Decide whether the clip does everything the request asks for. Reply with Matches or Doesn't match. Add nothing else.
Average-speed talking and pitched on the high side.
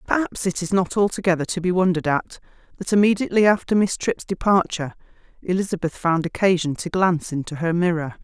Doesn't match